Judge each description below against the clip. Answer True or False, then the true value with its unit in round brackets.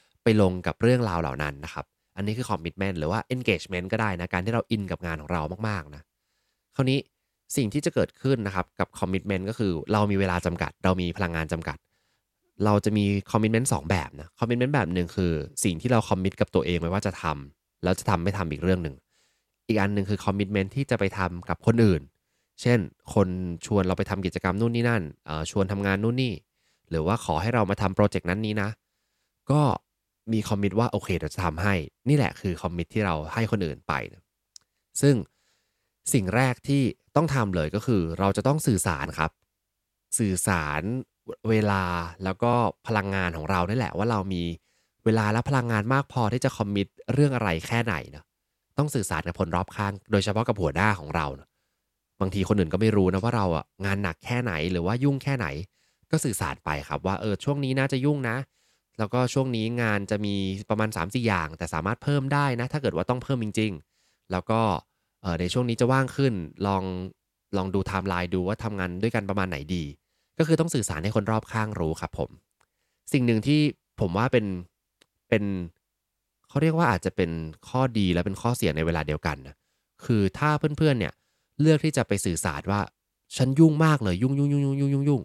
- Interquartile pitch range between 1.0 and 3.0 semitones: False (4.7 semitones)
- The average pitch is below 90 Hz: False (100 Hz)